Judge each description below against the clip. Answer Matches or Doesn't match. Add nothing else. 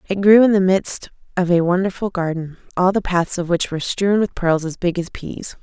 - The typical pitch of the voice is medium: Matches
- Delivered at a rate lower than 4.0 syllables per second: Doesn't match